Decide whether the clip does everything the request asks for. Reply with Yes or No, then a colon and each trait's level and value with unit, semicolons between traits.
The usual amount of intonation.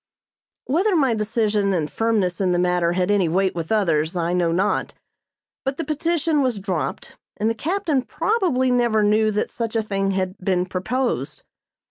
No: wide, 6.0 semitones